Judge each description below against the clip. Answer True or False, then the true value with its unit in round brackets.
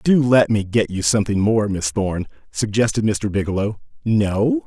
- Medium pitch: False (110 Hz)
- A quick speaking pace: False (165 wpm)